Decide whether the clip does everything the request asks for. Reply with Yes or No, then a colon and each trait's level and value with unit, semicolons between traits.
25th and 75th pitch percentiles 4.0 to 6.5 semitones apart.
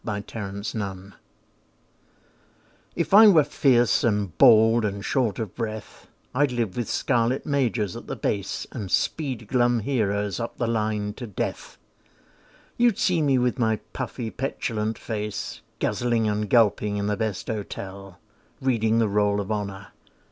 No: average, 3.0 semitones